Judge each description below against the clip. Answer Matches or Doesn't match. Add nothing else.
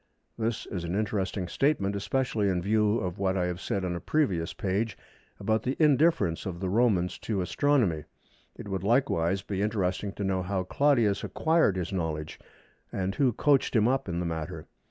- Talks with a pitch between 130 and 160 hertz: Doesn't match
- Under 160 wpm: Doesn't match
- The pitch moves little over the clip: Doesn't match